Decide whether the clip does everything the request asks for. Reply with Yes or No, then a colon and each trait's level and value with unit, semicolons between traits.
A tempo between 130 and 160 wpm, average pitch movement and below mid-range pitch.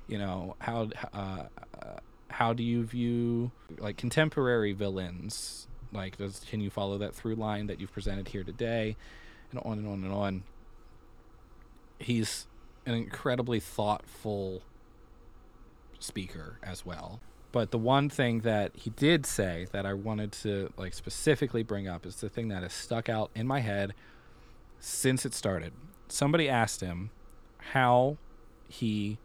Yes: average, 145 wpm; average, 3.2 semitones; low, 110 Hz